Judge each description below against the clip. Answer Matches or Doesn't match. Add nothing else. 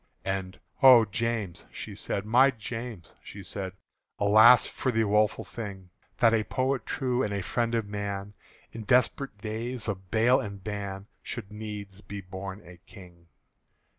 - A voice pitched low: Matches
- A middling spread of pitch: Matches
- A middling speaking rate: Matches